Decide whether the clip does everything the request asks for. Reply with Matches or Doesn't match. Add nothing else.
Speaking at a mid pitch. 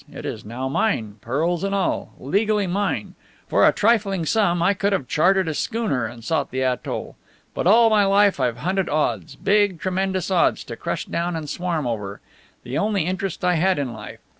Matches